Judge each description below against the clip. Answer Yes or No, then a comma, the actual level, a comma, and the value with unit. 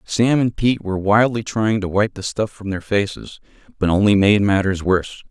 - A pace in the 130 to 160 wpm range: No, fast, 205 wpm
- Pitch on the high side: No, low, 105 Hz